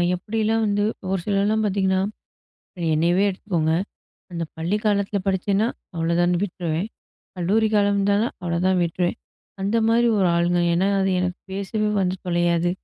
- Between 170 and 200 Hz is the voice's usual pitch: Yes, high, 190 Hz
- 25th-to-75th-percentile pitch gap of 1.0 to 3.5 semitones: Yes, average, 2.8 semitones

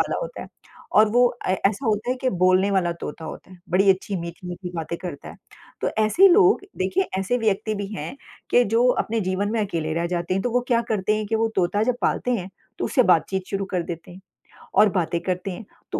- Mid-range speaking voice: No, high, 195 Hz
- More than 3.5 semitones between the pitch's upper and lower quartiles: Yes, average, 4.0 semitones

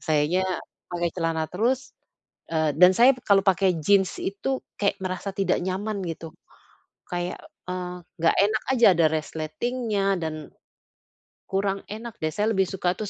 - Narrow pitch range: No, average, 3.2 semitones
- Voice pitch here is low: No, high, 190 Hz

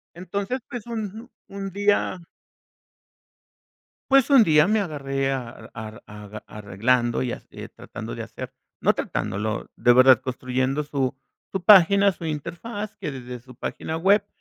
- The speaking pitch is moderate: Yes, medium, 150 Hz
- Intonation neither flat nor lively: No, wide, 8.0 semitones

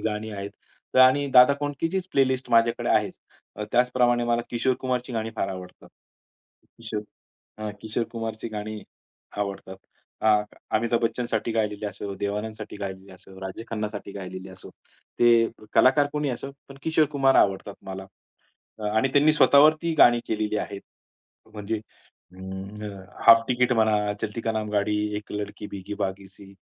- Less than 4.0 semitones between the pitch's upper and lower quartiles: Yes, average, 3.5 semitones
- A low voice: Yes, low, 110 Hz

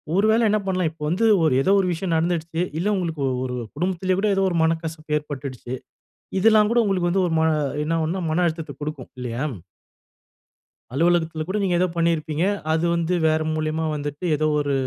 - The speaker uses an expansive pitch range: No, average, 2.9 semitones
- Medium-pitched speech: Yes, medium, 165 Hz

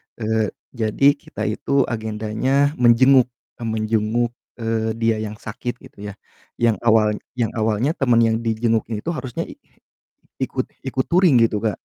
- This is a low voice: Yes, low, 115 Hz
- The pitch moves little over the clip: Yes, narrow, 2.1 semitones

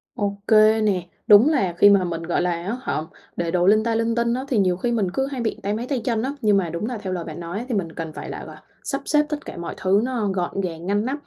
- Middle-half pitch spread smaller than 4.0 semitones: No, average, 4.8 semitones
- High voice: Yes, high, 205 Hz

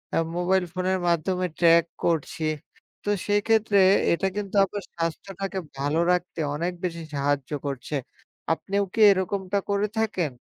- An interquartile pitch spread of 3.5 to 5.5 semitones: No, average, 3.1 semitones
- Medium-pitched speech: Yes, medium, 180 Hz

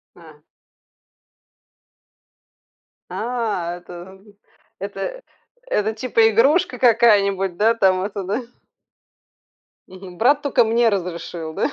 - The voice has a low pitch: No, high, 205 Hz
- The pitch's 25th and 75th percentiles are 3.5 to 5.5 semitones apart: Yes, average, 3.8 semitones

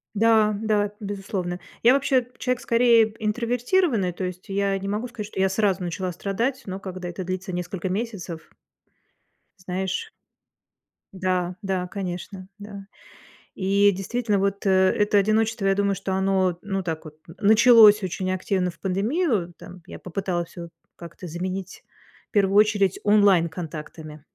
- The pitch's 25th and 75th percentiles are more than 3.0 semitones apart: No, narrow, 2.5 semitones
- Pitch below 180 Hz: No, high, 195 Hz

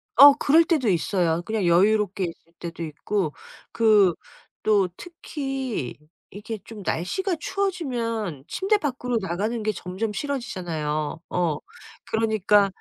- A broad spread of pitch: Yes, wide, 6.5 semitones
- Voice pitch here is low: No, high, 215 Hz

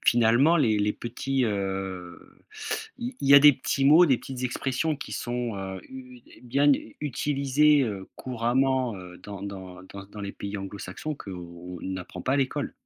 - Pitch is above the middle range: No, low, 120 Hz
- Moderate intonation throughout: No, wide, 5.9 semitones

